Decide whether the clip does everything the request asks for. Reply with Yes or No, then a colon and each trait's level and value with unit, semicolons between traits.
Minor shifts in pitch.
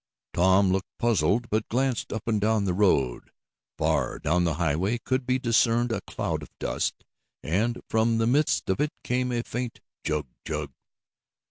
No: average, 5.0 semitones